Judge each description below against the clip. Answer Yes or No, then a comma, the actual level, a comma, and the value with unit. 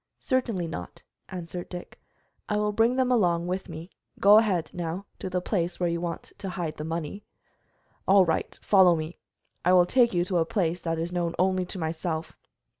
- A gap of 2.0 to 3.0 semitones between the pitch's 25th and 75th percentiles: Yes, narrow, 2.5 semitones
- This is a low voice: No, medium, 180 Hz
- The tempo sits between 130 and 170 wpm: No, average, 190 wpm